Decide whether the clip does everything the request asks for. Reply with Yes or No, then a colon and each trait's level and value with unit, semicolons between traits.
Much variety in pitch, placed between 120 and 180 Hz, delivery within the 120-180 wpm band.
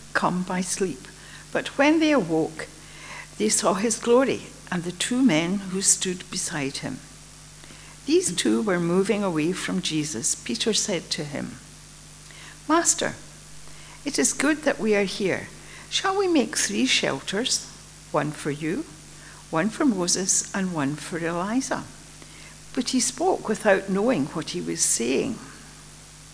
No: wide, 6.4 semitones; high, 190 Hz; average, 140 wpm